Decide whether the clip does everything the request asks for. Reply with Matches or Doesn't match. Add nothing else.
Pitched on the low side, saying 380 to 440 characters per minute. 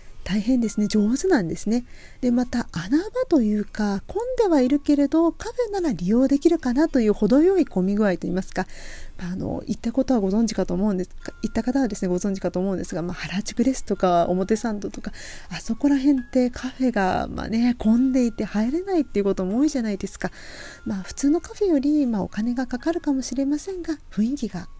Doesn't match